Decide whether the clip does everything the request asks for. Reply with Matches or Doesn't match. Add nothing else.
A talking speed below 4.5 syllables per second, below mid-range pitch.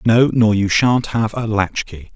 Matches